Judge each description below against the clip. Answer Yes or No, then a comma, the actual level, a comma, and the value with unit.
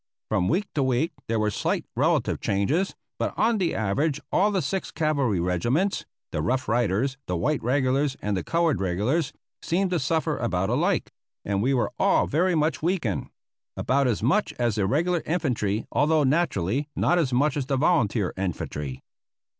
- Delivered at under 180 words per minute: Yes, average, 170 wpm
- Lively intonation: Yes, wide, 7.2 semitones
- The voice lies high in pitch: No, low, 135 Hz